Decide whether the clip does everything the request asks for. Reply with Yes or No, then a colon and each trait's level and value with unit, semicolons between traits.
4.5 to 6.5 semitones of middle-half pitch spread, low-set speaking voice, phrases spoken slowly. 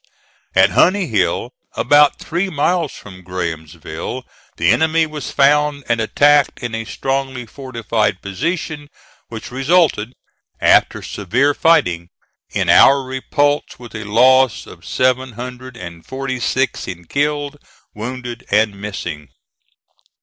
Yes: wide, 5.6 semitones; low, 130 Hz; slow, 120 wpm